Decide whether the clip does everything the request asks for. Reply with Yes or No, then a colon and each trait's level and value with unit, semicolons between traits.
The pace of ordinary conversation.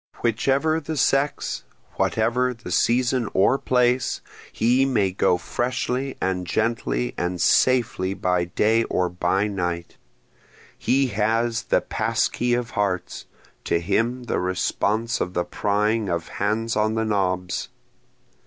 No: slow, 130 wpm